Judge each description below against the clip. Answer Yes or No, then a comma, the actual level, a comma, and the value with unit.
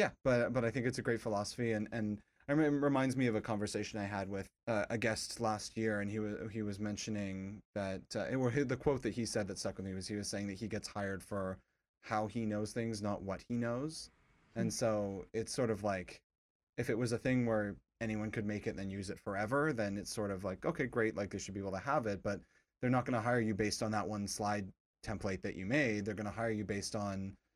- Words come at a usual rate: No, fast, 260 wpm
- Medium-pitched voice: No, low, 105 Hz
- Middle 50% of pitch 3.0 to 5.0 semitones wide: No, narrow, 2.4 semitones